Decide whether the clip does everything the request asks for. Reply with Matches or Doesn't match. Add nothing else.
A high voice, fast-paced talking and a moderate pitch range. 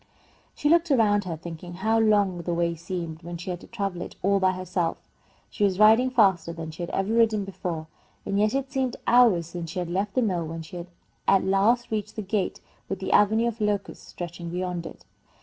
Matches